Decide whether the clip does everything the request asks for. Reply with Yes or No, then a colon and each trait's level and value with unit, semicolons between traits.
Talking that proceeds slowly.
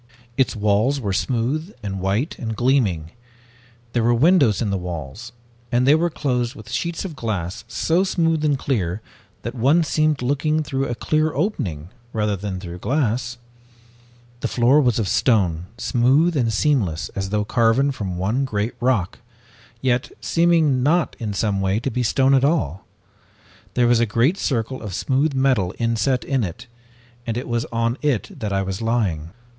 No: average, 170 wpm